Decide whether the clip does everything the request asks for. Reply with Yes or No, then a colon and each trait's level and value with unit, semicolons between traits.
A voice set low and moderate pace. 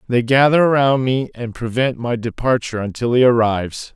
Yes: low, 120 Hz; average, 165 wpm